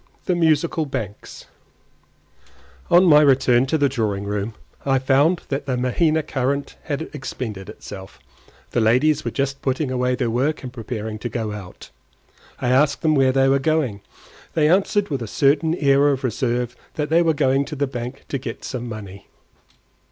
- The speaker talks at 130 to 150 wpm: No, average, 175 wpm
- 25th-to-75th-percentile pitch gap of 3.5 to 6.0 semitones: Yes, average, 3.8 semitones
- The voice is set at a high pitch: No, low, 135 Hz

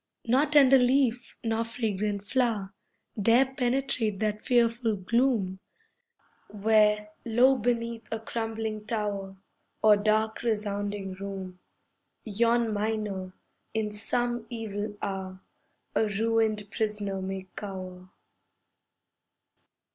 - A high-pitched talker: Yes, high, 215 Hz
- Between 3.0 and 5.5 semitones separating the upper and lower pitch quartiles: No, narrow, 2.5 semitones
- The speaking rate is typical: No, slow, 95 wpm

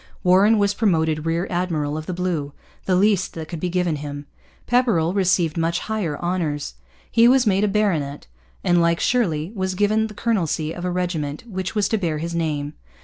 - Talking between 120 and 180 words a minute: No, average, 190 wpm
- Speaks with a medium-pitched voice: Yes, medium, 175 Hz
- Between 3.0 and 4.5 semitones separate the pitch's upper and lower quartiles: Yes, average, 4.2 semitones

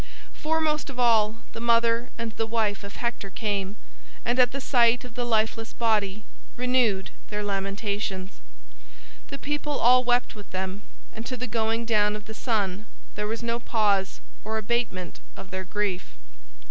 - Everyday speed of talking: Yes, average, 160 wpm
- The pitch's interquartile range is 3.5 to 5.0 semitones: No, average, 2.8 semitones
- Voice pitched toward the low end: No, high, 225 Hz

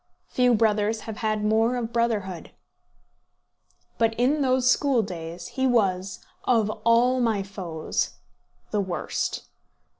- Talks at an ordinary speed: No, slow, 120 wpm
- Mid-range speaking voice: No, high, 220 Hz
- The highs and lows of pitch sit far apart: No, average, 3.7 semitones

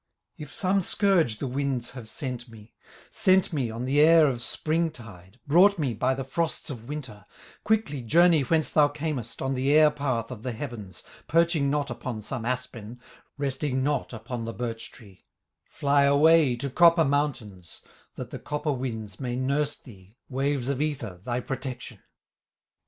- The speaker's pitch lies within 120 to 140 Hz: Yes, low, 135 Hz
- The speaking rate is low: No, average, 165 wpm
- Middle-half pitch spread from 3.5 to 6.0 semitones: Yes, average, 3.9 semitones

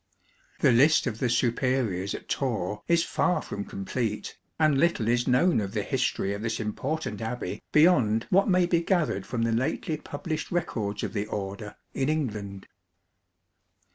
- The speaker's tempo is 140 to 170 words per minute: Yes, average, 160 wpm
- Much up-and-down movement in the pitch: Yes, wide, 6.6 semitones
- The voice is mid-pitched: No, low, 120 Hz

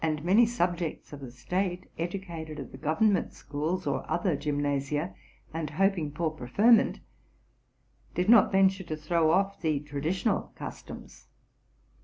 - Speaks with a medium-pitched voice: Yes, medium, 165 Hz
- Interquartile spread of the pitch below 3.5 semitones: No, average, 4.3 semitones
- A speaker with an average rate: No, slow, 130 wpm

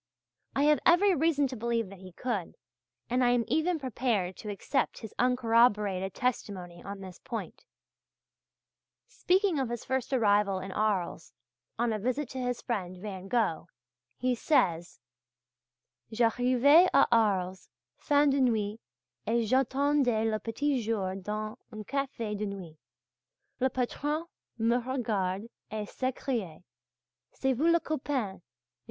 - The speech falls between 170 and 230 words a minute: No, slow, 135 wpm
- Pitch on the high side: Yes, high, 230 Hz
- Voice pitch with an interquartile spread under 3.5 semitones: No, average, 4.6 semitones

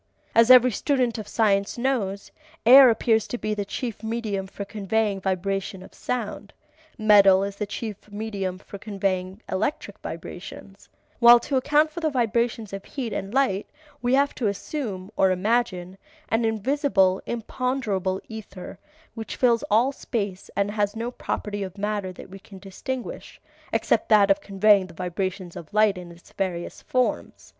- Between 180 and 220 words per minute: No, average, 155 wpm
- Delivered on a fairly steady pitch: No, average, 3.5 semitones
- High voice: Yes, high, 210 Hz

